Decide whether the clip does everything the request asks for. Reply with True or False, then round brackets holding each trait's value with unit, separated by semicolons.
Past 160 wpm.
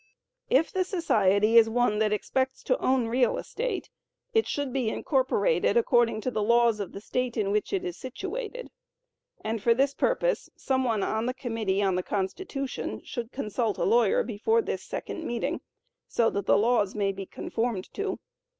True (175 wpm)